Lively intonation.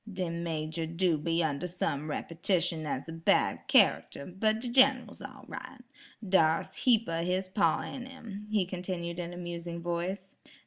No: average, 2.7 semitones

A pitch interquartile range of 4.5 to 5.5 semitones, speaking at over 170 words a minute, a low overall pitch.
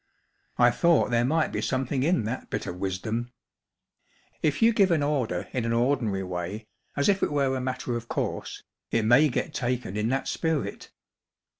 No: average, 4.1 semitones; average, 180 wpm; low, 125 Hz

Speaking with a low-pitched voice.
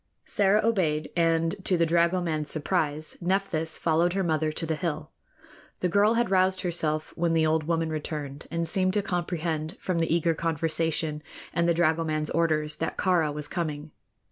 No: medium, 165 Hz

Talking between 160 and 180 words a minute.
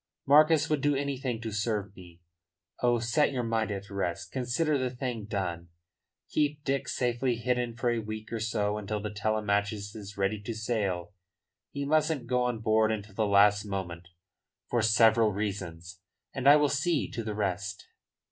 Yes: average, 170 wpm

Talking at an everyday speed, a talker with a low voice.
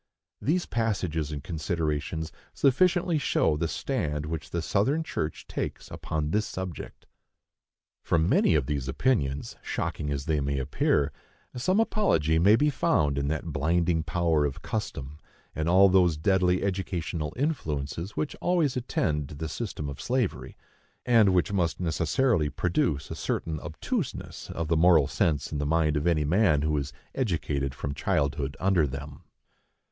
Yes: average, 150 wpm; very low, 80 Hz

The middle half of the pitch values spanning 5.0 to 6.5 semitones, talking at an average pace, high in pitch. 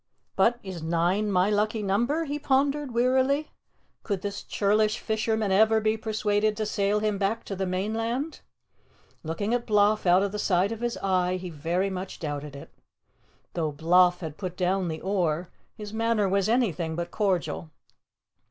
No: average, 3.4 semitones; average, 165 wpm; high, 200 Hz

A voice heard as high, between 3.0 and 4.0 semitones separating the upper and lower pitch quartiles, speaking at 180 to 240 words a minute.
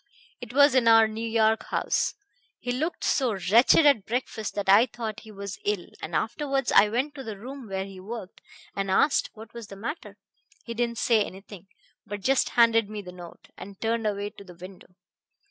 Yes: high, 220 Hz; average, 3.3 semitones; average, 195 wpm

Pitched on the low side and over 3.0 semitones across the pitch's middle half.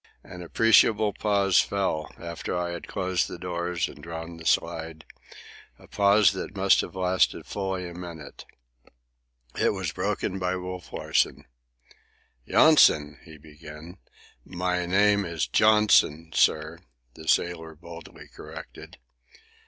No: very low, 90 Hz; average, 2.7 semitones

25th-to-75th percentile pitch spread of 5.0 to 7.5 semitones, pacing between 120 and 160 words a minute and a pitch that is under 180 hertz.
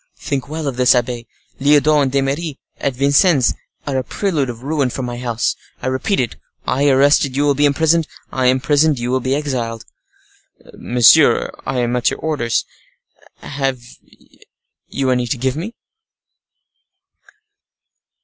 No: average, 2.7 semitones; average, 140 wpm; low, 135 Hz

